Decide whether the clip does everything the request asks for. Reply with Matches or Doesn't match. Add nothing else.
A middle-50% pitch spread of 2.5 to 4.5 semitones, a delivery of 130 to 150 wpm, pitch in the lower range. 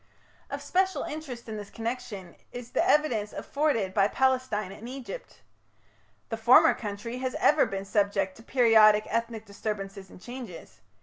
Doesn't match